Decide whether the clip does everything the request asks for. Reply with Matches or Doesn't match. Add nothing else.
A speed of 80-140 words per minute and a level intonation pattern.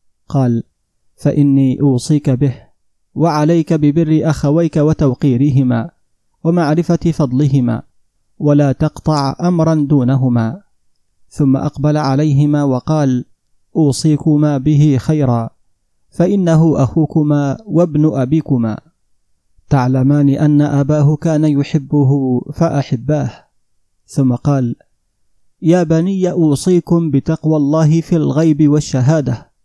Doesn't match